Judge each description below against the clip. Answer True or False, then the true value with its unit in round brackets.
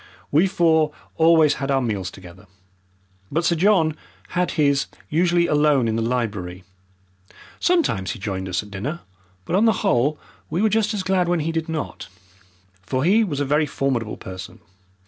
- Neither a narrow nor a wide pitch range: False (7.1 semitones)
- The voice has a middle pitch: True (150 Hz)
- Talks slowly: False (170 wpm)